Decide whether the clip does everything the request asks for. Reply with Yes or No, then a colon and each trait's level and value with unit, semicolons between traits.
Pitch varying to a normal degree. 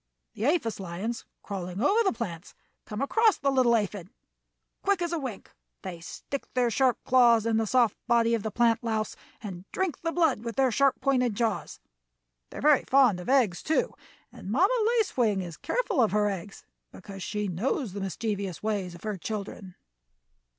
Yes: average, 5.0 semitones